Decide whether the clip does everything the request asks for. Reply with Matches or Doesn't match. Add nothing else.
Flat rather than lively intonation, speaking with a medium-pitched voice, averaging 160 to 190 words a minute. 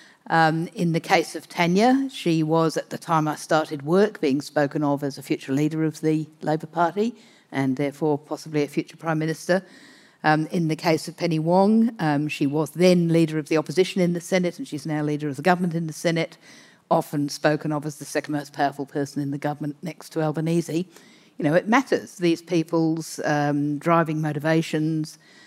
Doesn't match